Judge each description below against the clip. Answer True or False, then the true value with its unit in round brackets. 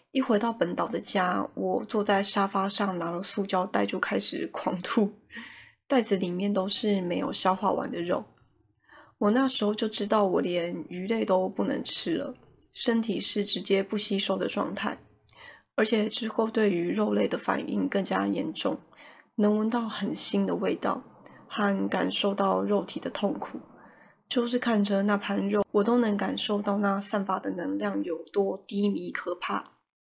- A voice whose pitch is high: True (205 Hz)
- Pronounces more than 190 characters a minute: True (240 characters per minute)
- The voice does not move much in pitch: True (2.3 semitones)